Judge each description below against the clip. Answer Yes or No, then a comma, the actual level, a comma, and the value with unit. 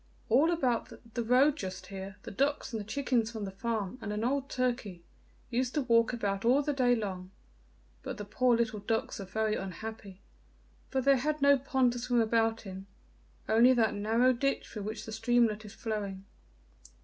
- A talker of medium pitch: No, high, 230 Hz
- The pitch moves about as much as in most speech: Yes, average, 3.4 semitones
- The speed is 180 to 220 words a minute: Yes, average, 185 wpm